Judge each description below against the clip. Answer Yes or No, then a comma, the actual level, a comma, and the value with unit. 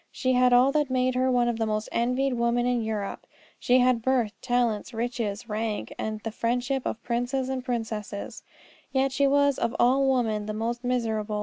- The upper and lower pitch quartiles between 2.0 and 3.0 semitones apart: Yes, narrow, 2.4 semitones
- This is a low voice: No, high, 245 Hz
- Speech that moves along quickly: No, average, 195 wpm